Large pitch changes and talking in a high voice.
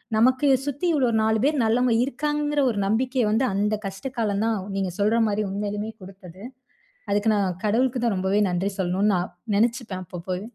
No: average, 4.1 semitones; high, 210 Hz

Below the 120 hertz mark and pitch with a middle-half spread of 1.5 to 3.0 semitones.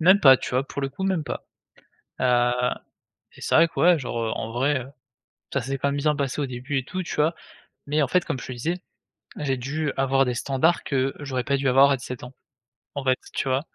No: low, 135 Hz; narrow, 2.6 semitones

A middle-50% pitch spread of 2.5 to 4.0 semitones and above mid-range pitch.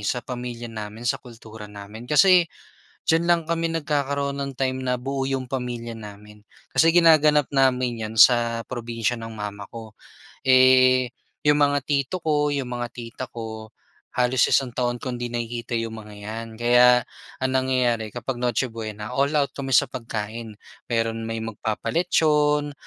No: average, 3.3 semitones; low, 125 Hz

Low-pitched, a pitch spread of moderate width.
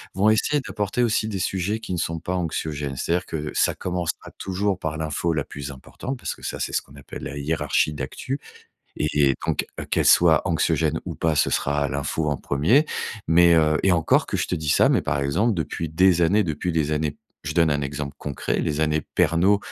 Yes: very low, 80 Hz; average, 3.7 semitones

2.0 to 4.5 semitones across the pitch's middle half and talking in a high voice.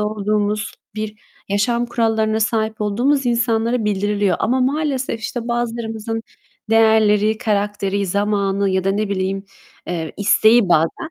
Yes: narrow, 2.4 semitones; high, 215 Hz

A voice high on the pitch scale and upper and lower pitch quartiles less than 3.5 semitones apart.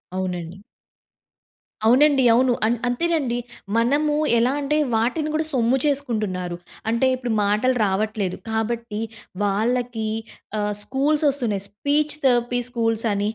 No: high, 235 Hz; average, 4.0 semitones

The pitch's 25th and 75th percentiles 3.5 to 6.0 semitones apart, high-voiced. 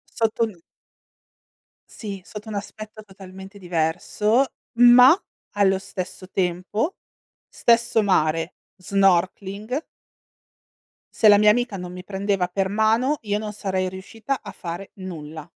No: average, 2.9 semitones; high, 200 Hz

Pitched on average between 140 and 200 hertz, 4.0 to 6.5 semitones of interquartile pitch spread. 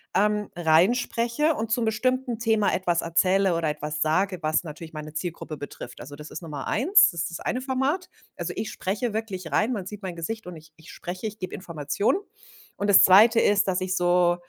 Yes: medium, 185 Hz; average, 5.2 semitones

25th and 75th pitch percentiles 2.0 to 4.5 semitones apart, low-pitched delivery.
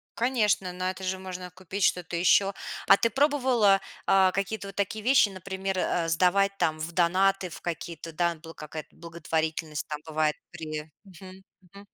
No: average, 3.1 semitones; medium, 185 Hz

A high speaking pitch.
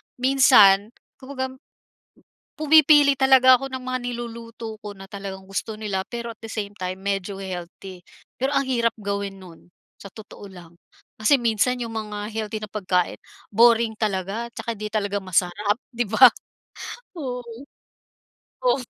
Yes: high, 220 Hz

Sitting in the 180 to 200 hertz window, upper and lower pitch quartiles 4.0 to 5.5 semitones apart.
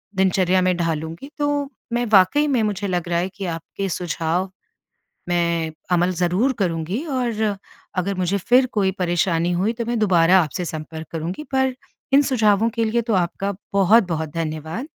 Yes: medium, 185 Hz; average, 4.8 semitones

